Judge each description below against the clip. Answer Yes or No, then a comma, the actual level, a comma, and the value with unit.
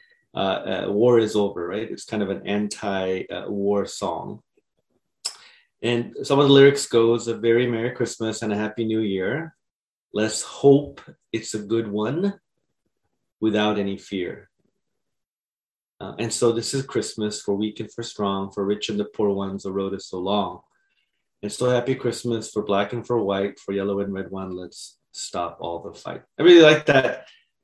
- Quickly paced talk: No, average, 180 wpm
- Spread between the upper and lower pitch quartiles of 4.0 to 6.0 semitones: No, average, 3.0 semitones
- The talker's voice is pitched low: Yes, low, 110 Hz